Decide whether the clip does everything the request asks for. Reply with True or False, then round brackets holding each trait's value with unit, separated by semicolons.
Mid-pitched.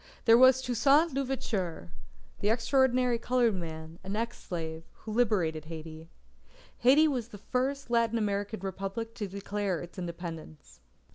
False (210 Hz)